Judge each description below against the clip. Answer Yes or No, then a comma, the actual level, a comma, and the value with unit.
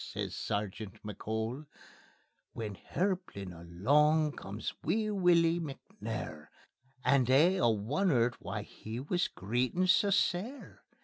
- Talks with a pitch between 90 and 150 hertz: Yes, low, 135 Hz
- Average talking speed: No, slow, 110 wpm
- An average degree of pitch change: No, wide, 8.6 semitones